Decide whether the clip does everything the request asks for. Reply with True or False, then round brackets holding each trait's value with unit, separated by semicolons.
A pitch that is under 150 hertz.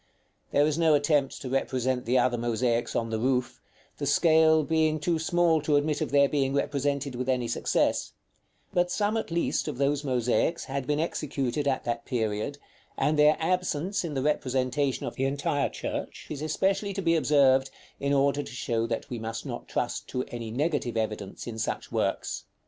True (140 Hz)